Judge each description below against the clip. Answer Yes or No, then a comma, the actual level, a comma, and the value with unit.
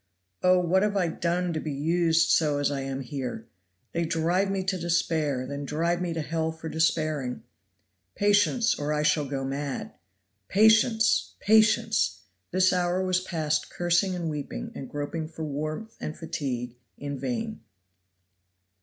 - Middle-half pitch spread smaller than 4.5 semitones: Yes, average, 4.0 semitones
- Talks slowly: No, average, 155 wpm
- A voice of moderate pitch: Yes, medium, 165 Hz